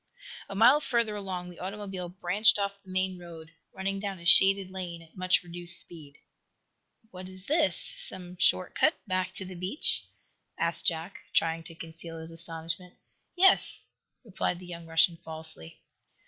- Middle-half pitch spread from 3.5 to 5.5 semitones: No, average, 2.7 semitones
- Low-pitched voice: No, medium, 180 Hz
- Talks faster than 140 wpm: Yes, average, 160 wpm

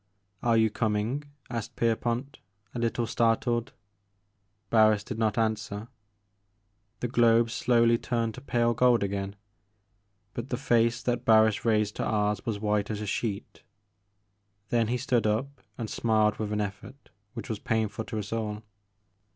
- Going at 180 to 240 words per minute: No, average, 150 wpm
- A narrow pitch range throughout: Yes, narrow, 1.9 semitones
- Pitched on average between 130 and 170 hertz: No, low, 115 Hz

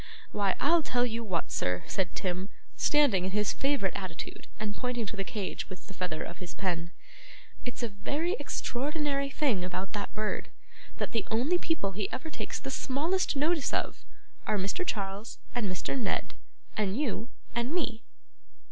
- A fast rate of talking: No, average, 170 wpm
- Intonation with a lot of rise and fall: Yes, wide, 6.2 semitones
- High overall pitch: Yes, high, 220 Hz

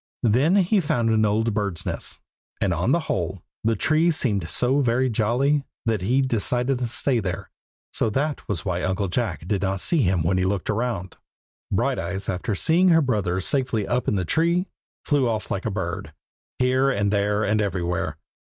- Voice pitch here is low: Yes, low, 110 Hz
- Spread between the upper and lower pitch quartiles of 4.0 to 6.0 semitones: Yes, average, 5.2 semitones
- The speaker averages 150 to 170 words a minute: No, average, 185 wpm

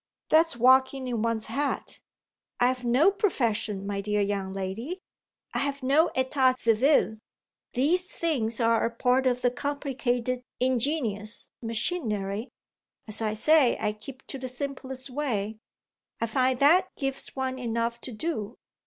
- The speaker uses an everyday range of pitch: Yes, average, 3.6 semitones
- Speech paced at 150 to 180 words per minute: No, slow, 135 wpm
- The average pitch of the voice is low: No, very high, 250 Hz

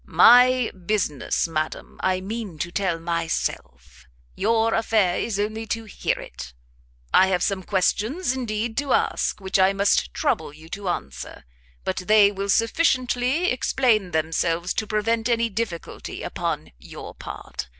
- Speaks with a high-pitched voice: Yes, high, 205 Hz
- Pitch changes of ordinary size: Yes, average, 4.4 semitones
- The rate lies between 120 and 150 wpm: Yes, average, 140 wpm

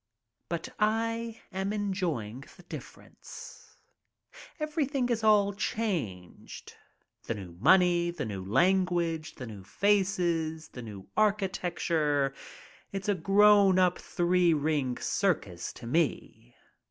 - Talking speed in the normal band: No, slow, 115 wpm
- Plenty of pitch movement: Yes, wide, 6.0 semitones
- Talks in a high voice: No, medium, 175 Hz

